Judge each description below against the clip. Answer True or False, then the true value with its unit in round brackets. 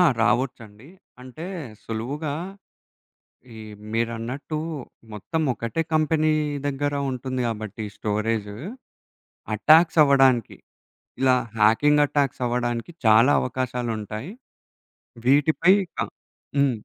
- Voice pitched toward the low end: True (130 Hz)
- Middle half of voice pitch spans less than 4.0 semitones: False (4.3 semitones)